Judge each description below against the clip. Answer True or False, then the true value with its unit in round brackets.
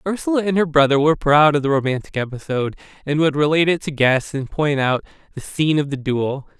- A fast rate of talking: True (220 wpm)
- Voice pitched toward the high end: False (150 Hz)